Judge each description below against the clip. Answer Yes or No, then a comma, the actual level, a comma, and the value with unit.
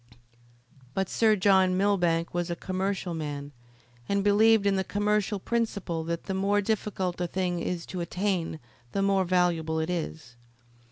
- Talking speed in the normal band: Yes, average, 155 wpm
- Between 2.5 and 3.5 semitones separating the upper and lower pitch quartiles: Yes, average, 2.9 semitones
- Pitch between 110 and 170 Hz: No, medium, 185 Hz